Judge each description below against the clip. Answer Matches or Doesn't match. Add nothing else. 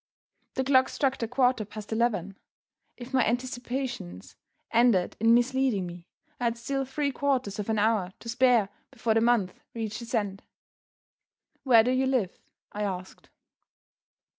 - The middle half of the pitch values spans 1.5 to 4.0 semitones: Matches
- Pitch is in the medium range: Doesn't match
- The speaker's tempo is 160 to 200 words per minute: Doesn't match